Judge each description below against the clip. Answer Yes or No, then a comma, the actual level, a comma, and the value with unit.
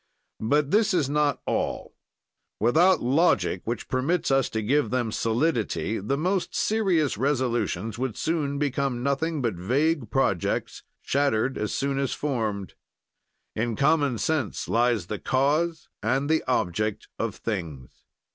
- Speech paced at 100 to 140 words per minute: Yes, slow, 135 wpm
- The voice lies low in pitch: Yes, low, 130 Hz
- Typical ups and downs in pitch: Yes, average, 5.0 semitones